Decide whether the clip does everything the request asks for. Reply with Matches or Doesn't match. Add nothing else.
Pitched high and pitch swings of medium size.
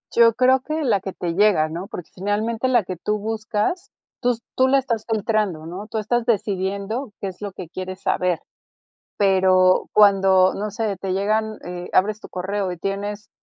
Matches